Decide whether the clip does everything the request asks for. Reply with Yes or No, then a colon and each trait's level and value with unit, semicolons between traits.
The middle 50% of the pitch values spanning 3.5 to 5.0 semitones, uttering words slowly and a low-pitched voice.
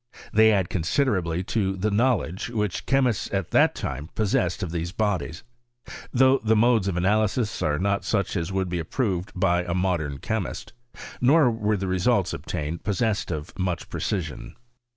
No: average, 3.8 semitones; average, 170 wpm; very low, 95 Hz